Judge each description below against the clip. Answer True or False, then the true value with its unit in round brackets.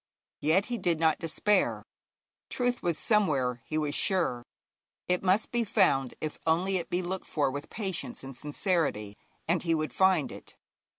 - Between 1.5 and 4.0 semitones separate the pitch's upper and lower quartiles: False (4.4 semitones)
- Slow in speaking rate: False (165 wpm)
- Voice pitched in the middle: True (170 Hz)